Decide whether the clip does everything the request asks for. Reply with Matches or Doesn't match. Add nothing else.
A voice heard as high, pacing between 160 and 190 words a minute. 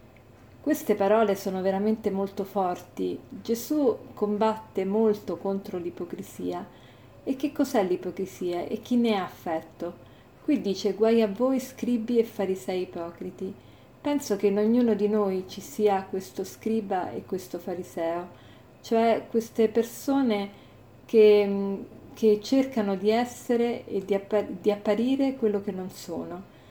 Doesn't match